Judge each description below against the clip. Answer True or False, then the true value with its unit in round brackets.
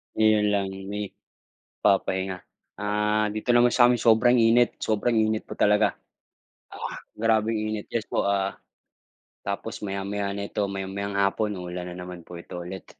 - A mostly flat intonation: True (2.1 semitones)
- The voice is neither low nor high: False (105 Hz)